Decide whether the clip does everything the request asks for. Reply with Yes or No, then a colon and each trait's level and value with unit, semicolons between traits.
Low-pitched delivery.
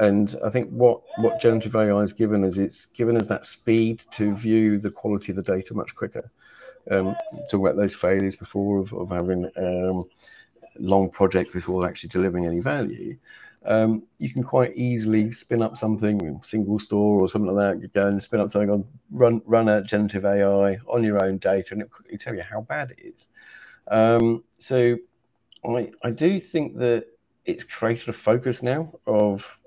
Yes: low, 105 Hz